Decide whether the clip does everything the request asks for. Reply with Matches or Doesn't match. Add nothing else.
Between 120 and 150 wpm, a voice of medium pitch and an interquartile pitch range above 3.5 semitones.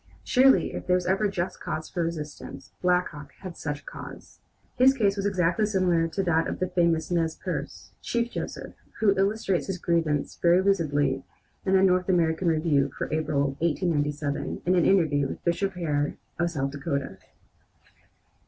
Doesn't match